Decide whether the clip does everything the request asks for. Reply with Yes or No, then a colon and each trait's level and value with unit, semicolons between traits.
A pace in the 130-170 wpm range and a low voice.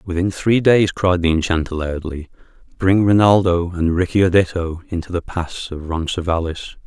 Yes: average, 150 wpm; very low, 90 Hz